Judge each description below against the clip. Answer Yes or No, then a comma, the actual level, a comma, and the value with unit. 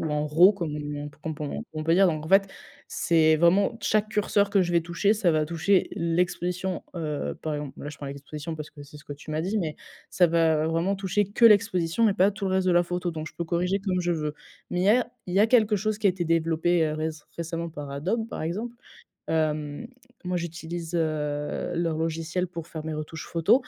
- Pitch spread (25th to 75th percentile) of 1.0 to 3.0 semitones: No, average, 3.4 semitones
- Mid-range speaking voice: Yes, medium, 170 Hz